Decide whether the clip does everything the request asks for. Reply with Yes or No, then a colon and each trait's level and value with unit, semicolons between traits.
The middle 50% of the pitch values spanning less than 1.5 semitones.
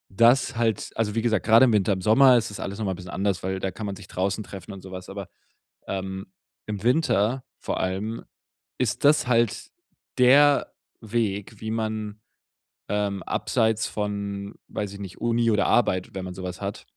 No: average, 2.9 semitones